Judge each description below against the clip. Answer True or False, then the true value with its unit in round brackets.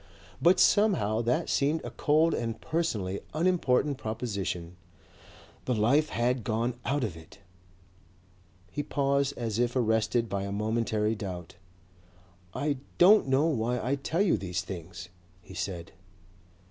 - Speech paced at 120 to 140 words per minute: True (135 wpm)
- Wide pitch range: True (5.8 semitones)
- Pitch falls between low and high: False (120 Hz)